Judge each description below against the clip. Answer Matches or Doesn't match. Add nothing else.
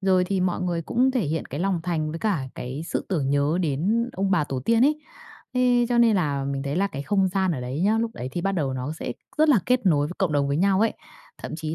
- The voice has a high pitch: Doesn't match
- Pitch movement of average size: Doesn't match